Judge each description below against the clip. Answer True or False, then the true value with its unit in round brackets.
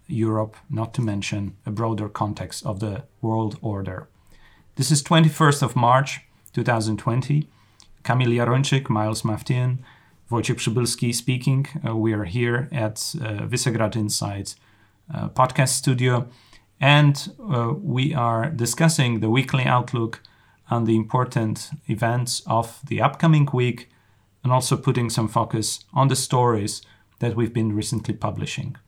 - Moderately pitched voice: False (120 Hz)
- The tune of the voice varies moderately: True (3.4 semitones)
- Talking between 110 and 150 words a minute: True (135 wpm)